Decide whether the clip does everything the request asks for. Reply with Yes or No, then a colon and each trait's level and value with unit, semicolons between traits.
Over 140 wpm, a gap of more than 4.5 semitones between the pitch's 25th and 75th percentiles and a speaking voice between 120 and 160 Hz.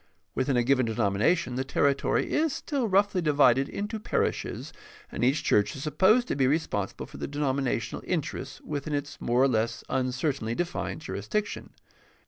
Yes: average, 160 wpm; average, 5.1 semitones; medium, 140 Hz